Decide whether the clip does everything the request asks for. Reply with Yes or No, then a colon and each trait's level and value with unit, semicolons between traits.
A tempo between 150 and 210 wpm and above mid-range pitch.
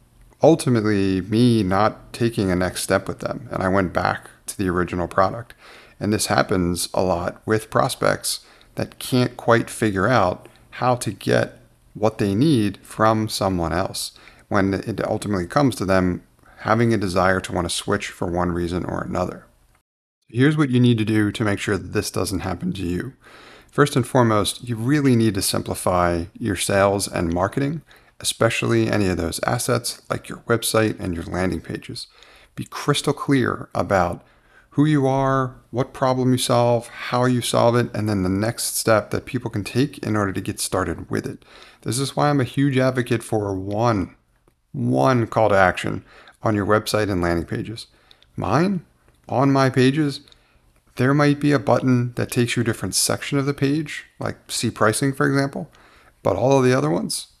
No: average, 185 wpm; low, 110 Hz